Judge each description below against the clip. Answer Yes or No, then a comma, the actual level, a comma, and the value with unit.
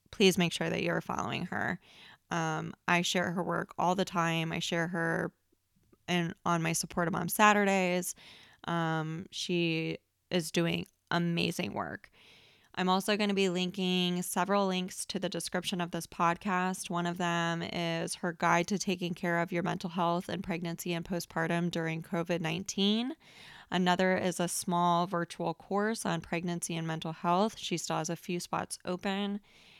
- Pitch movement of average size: No, narrow, 1.5 semitones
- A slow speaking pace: No, average, 165 wpm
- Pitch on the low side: No, medium, 175 Hz